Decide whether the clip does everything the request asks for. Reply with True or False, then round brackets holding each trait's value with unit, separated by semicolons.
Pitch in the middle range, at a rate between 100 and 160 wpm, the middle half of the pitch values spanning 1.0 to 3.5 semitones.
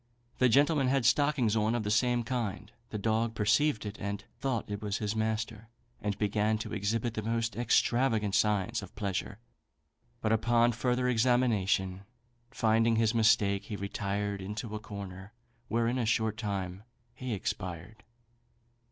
False (110 Hz; 150 wpm; 2.5 semitones)